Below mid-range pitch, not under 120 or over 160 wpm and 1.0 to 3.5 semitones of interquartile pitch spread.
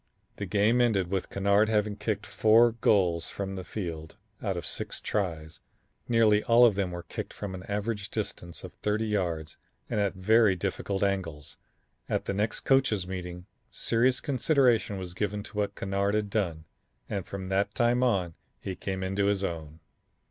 No: low, 100 Hz; average, 170 wpm; average, 2.8 semitones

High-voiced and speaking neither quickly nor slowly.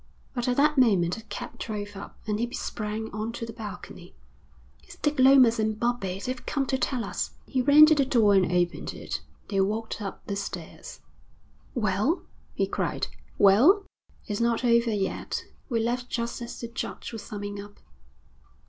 Yes: high, 230 Hz; average, 175 wpm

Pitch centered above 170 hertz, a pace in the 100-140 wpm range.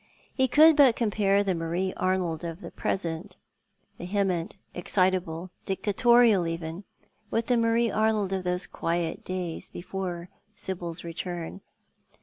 Yes: medium, 185 Hz; slow, 135 wpm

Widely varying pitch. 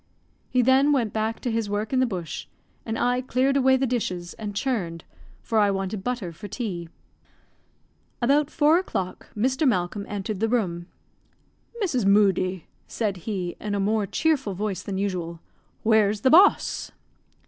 No: average, 4.8 semitones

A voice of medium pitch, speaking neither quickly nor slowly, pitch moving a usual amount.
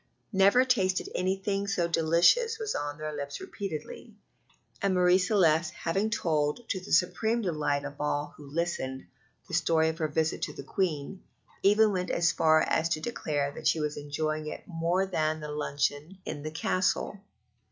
Yes: medium, 165 Hz; average, 170 wpm; average, 4.1 semitones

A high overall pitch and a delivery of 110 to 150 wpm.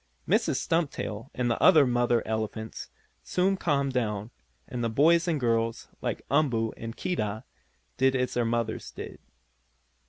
No: low, 120 Hz; average, 145 wpm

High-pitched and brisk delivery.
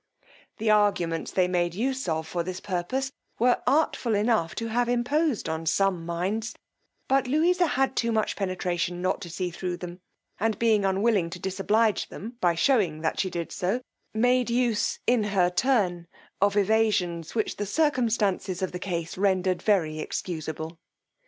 No: high, 195 Hz; average, 160 wpm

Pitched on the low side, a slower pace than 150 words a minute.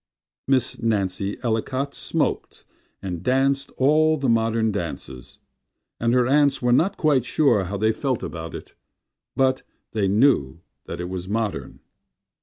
Yes: low, 115 Hz; average, 140 wpm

